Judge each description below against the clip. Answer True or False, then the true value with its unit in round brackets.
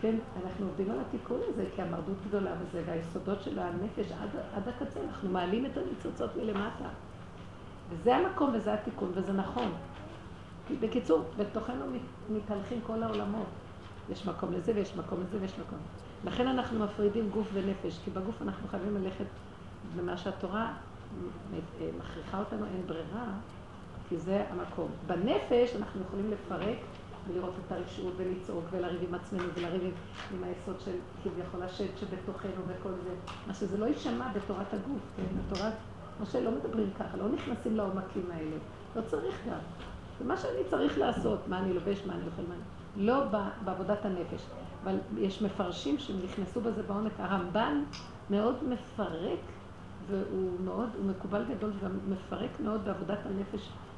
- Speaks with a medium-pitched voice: False (195 Hz)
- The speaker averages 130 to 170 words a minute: True (150 wpm)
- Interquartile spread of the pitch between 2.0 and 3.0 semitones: True (2.7 semitones)